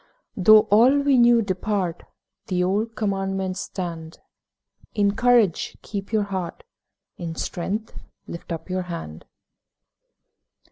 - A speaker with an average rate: No, slow, 110 wpm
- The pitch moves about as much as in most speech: Yes, average, 3.3 semitones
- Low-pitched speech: No, high, 195 Hz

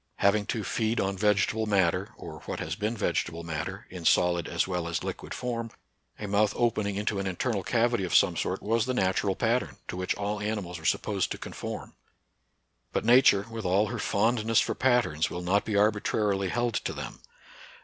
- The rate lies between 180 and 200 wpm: Yes, average, 190 wpm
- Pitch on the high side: No, low, 105 Hz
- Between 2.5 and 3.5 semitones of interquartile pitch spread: Yes, average, 3.2 semitones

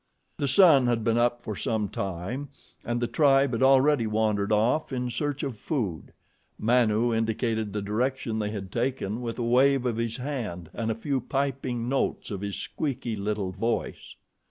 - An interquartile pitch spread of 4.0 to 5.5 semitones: No, average, 3.6 semitones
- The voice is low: Yes, low, 120 Hz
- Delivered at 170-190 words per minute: Yes, average, 175 wpm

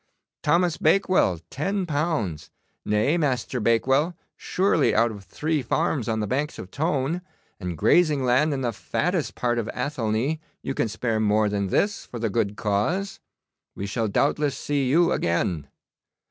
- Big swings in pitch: Yes, wide, 6.6 semitones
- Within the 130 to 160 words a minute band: Yes, average, 155 wpm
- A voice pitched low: Yes, low, 130 Hz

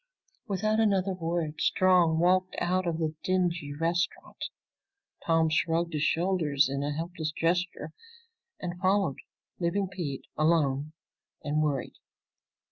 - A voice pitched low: No, medium, 170 Hz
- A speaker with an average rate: No, slow, 120 wpm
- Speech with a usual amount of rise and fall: Yes, average, 3.0 semitones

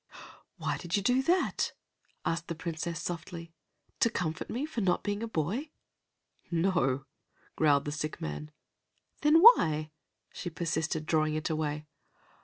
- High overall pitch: No, medium, 165 Hz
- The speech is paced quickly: No, average, 140 wpm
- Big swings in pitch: No, average, 4.8 semitones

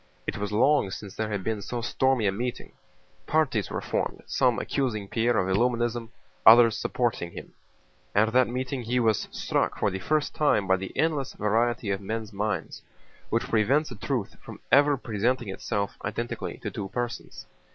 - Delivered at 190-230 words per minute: No, average, 170 wpm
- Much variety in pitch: No, average, 3.5 semitones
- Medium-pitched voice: No, low, 115 Hz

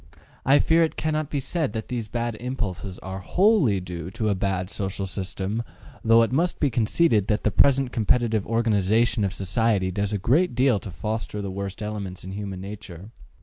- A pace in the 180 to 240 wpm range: Yes, average, 190 wpm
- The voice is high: No, low, 110 Hz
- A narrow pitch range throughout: No, average, 3.9 semitones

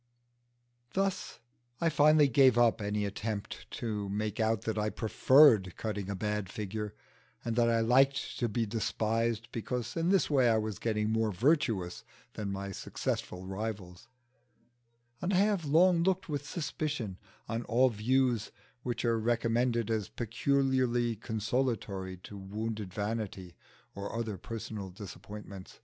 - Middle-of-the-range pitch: No, low, 115 Hz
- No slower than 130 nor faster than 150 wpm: Yes, average, 140 wpm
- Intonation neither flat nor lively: Yes, average, 3.5 semitones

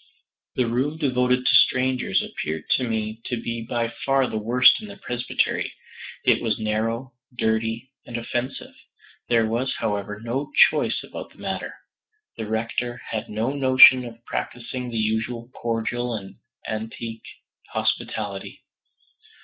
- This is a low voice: Yes, low, 115 Hz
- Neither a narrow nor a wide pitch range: No, narrow, 2.2 semitones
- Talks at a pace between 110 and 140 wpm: Yes, slow, 135 wpm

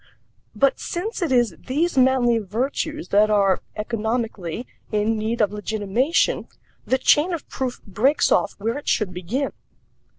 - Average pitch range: Yes, average, 4.4 semitones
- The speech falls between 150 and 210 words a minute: No, average, 140 wpm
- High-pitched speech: Yes, high, 230 Hz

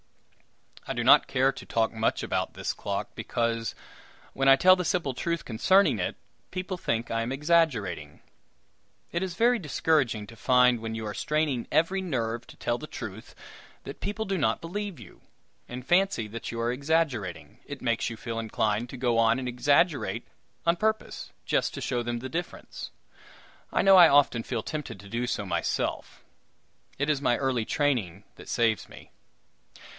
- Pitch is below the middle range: Yes, low, 130 Hz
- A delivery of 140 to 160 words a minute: No, average, 175 wpm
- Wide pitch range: Yes, wide, 6.4 semitones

